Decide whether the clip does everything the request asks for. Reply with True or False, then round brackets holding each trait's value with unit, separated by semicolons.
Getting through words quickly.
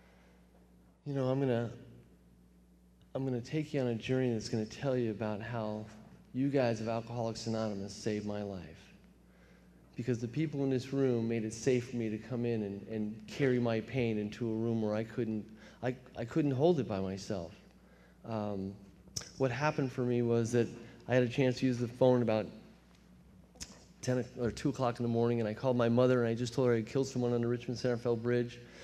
True (210 wpm)